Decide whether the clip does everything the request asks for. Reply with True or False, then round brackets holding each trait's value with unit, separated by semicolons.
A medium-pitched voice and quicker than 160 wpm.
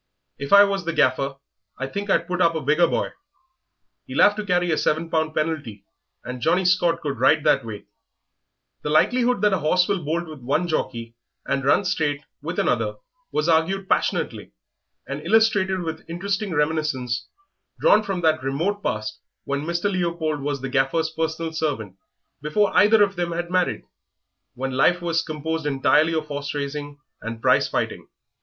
True (160 Hz; 170 wpm)